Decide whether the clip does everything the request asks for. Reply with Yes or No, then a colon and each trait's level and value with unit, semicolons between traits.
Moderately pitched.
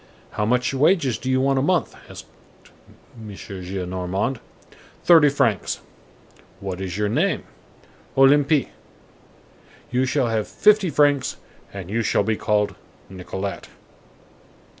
No: low, 120 Hz